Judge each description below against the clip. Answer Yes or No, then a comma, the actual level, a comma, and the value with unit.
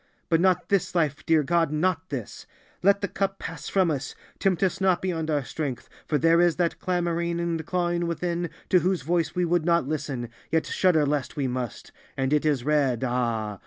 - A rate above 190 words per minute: Yes, average, 200 wpm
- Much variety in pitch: No, average, 3.3 semitones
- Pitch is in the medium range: Yes, medium, 165 Hz